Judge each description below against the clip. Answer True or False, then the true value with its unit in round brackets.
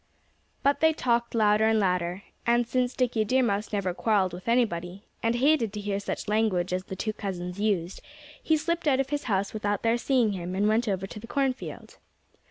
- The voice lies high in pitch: True (215 Hz)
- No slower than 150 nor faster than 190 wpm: False (200 wpm)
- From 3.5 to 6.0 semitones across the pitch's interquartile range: True (3.9 semitones)